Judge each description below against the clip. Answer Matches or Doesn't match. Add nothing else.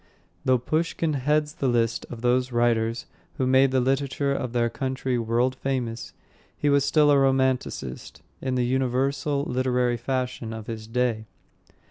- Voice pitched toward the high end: Doesn't match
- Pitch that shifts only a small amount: Matches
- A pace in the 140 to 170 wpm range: Matches